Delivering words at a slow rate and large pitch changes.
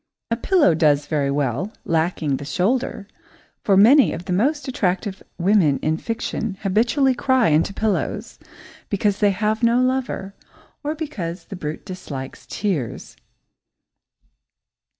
Yes: slow, 130 wpm; wide, 6.4 semitones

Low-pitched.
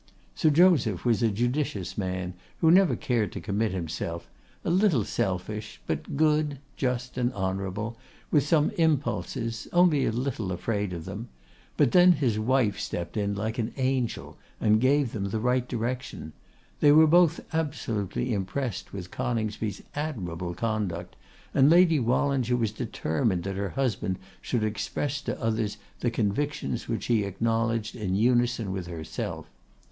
Yes: low, 115 Hz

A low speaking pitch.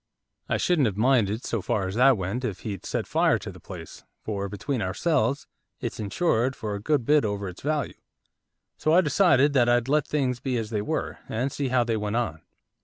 Yes: low, 120 Hz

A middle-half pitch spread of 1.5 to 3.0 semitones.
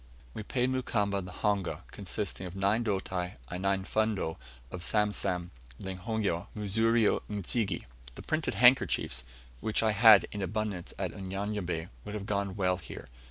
Yes: average, 2.7 semitones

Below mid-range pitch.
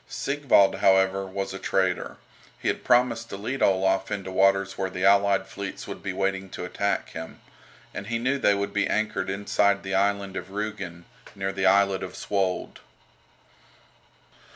Yes: low, 100 Hz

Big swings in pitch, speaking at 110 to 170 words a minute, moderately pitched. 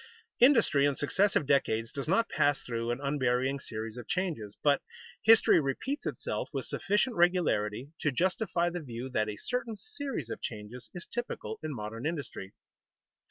Yes: wide, 7.8 semitones; average, 160 wpm; medium, 145 Hz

